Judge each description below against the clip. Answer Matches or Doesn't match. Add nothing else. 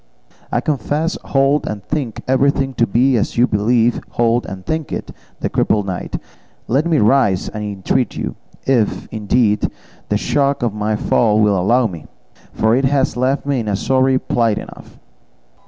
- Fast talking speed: Doesn't match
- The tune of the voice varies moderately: Matches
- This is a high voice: Doesn't match